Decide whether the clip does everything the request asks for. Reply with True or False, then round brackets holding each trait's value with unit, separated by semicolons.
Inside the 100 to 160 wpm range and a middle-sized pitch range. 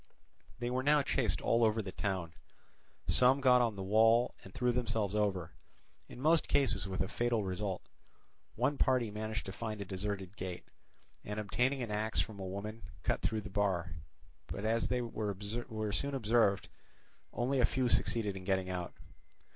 False (170 wpm; 3.7 semitones)